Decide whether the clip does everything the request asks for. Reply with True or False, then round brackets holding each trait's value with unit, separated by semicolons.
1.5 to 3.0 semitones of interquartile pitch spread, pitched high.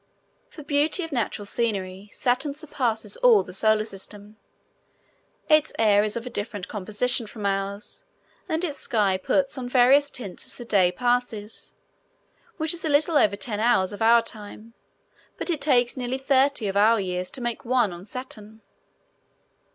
False (4.8 semitones; 230 Hz)